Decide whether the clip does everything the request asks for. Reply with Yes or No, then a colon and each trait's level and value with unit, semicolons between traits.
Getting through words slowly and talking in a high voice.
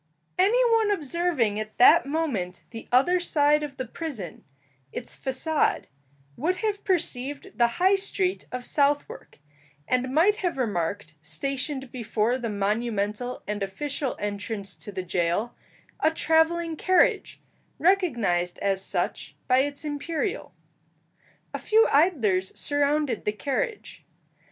Yes: slow, 125 wpm; very high, 275 Hz